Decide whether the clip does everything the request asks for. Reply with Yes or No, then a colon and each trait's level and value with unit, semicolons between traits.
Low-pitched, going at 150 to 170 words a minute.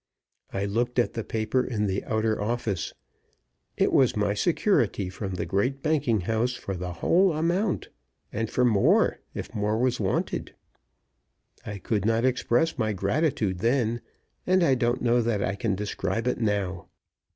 Yes: low, 115 Hz; average, 160 wpm